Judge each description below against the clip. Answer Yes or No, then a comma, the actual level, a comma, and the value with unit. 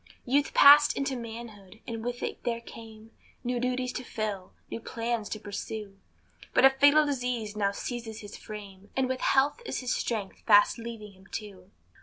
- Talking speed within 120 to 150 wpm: No, average, 175 wpm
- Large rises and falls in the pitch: No, average, 3.2 semitones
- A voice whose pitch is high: Yes, high, 230 Hz